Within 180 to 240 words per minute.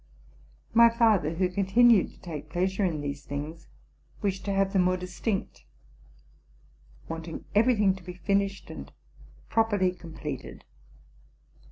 No: slow, 135 wpm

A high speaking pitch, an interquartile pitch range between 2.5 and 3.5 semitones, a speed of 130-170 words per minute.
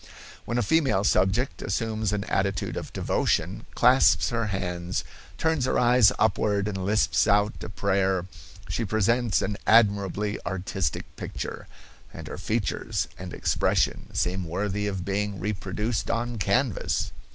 No: low, 105 Hz; average, 3.1 semitones; slow, 135 wpm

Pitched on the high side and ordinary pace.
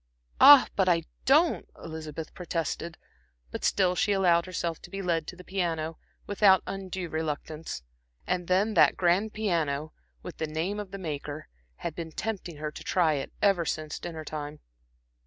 No: medium, 170 Hz; average, 165 wpm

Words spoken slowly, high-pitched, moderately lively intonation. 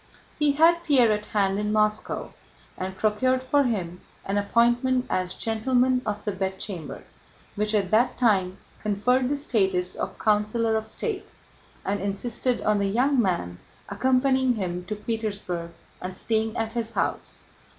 No: average, 150 wpm; high, 215 Hz; average, 4.1 semitones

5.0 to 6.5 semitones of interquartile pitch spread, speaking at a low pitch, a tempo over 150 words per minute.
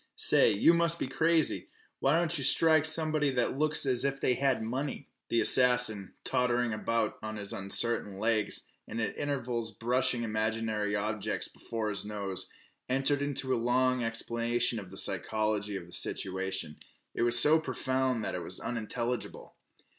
No: average, 3.9 semitones; low, 120 Hz; average, 160 wpm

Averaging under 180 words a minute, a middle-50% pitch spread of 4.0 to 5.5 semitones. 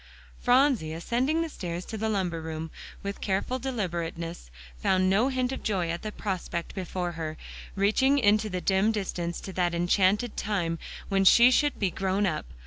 Yes: average, 170 wpm; average, 4.3 semitones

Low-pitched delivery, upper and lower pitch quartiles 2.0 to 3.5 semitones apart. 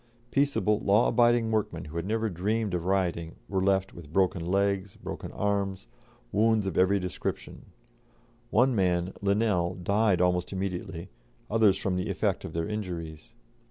Yes: very low, 95 Hz; average, 3.0 semitones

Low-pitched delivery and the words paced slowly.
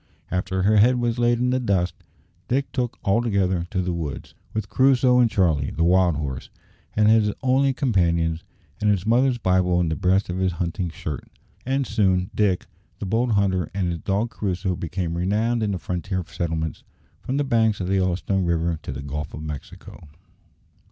No: very low, 95 Hz; average, 185 wpm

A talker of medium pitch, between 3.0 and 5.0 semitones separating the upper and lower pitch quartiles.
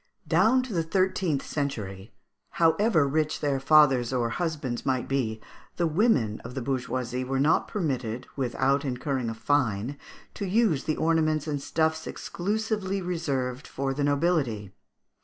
Yes: medium, 145 Hz; average, 4.4 semitones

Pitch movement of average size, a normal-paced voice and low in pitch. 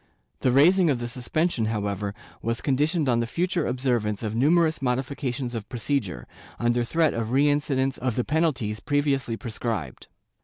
Yes: average, 4.0 semitones; average, 155 wpm; low, 125 Hz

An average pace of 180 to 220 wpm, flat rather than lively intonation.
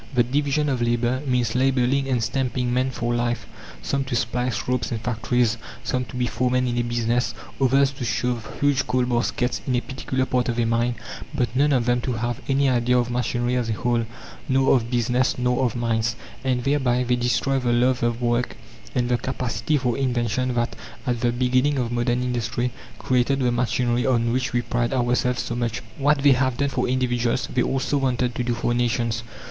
Yes: average, 200 wpm; narrow, 1.4 semitones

